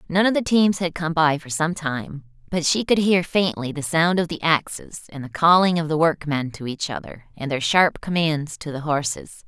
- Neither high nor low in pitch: Yes, medium, 160 Hz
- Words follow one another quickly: Yes, fast, 230 wpm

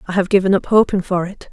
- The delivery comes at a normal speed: No, fast, 275 wpm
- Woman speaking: Yes, female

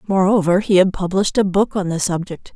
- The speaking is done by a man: No, female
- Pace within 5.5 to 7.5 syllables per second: Yes, 5.9 syllables/s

